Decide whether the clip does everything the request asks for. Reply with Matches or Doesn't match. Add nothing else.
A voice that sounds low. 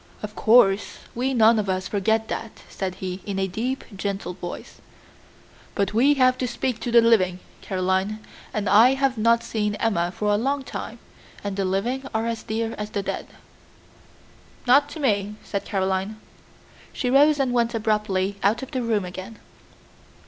Doesn't match